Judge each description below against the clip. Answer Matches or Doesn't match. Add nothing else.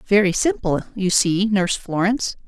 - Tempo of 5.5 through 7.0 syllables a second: Doesn't match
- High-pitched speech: Matches